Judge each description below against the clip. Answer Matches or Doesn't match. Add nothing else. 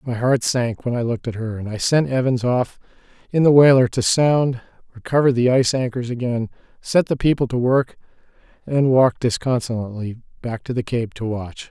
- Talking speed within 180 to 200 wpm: Matches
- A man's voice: Matches